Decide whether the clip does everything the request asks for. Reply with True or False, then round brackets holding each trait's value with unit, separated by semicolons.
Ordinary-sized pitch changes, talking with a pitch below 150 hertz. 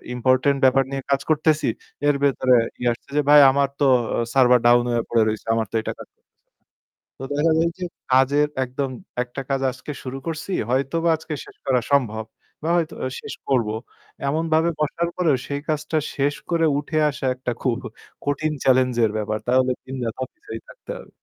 True (3.4 semitones; 135 Hz)